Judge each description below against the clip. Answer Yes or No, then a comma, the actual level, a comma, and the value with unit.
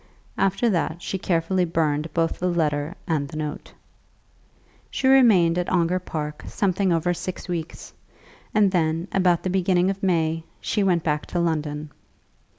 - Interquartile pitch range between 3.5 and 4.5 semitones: No, average, 2.8 semitones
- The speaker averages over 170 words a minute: No, average, 155 wpm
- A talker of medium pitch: Yes, medium, 170 Hz